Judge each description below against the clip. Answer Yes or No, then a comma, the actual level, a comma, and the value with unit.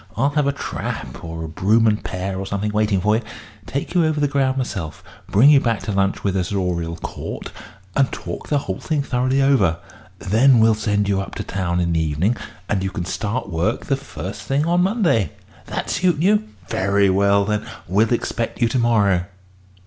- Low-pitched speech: Yes, low, 105 Hz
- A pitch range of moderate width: No, wide, 5.9 semitones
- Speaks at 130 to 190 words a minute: No, fast, 205 wpm